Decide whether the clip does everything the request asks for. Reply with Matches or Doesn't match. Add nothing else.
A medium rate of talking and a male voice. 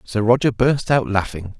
Matches